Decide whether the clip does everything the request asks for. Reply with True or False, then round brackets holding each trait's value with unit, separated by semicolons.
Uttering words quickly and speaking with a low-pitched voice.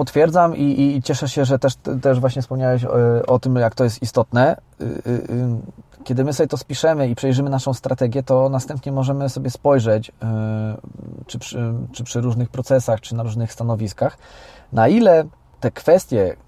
True (180 wpm; 130 Hz)